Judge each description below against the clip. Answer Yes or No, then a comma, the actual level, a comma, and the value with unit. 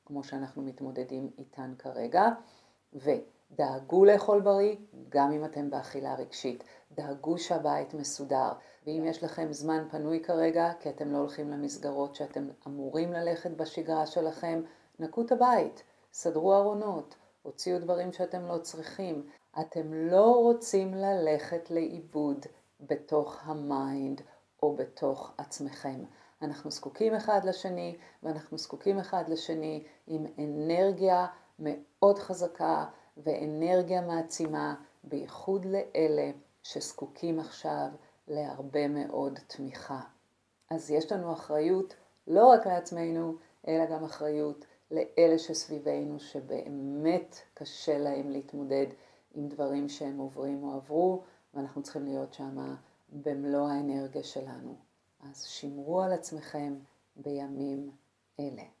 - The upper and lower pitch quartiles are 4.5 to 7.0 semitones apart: No, average, 3.2 semitones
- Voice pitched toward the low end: No, medium, 155 Hz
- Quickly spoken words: No, average, 110 wpm